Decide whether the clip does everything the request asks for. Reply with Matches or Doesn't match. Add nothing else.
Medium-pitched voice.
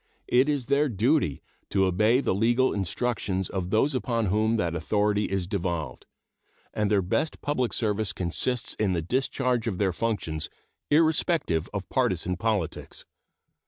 Doesn't match